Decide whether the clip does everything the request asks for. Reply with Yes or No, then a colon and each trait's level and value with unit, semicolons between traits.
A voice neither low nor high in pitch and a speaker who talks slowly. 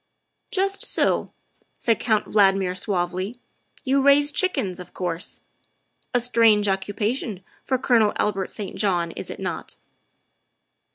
No: high, 210 Hz; slow, 130 wpm